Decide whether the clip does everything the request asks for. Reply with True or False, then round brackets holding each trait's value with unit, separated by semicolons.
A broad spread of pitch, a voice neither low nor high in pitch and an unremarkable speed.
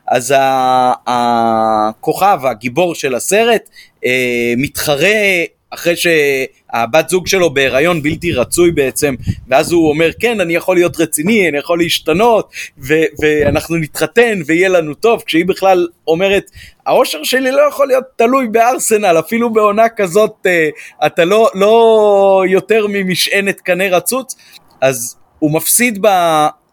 True (5.8 semitones; 170 Hz; 120 wpm)